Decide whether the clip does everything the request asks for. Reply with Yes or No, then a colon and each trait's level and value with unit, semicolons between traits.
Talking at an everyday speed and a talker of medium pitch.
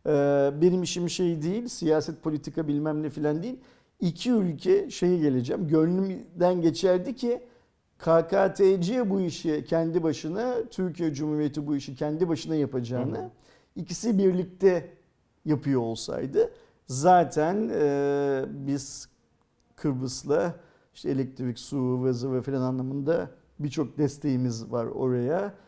Yes: average, 110 wpm; medium, 160 Hz